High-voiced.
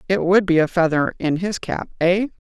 No: medium, 180 Hz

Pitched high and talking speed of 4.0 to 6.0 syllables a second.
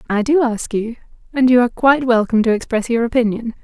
No: high, 235 Hz; 6.6 syllables/s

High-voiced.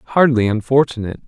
No: low, 120 Hz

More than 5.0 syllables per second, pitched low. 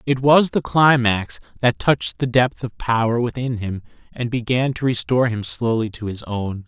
No: 4.8 syllables/s; low, 120 Hz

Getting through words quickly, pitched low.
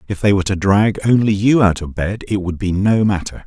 Yes: fast, 260 wpm; low, 100 Hz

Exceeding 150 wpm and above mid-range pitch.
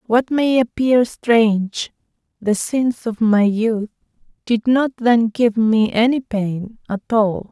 No: average, 145 wpm; high, 225 Hz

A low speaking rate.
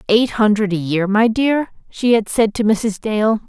No: fast, 205 wpm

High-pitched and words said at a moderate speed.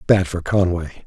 No: very low, 90 Hz; average, 170 wpm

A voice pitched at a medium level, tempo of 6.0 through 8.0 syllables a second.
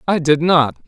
No: medium, 155 Hz; 4.6 syllables/s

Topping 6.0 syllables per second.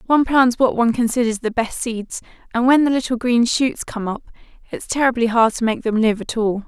No: 5.6 syllables/s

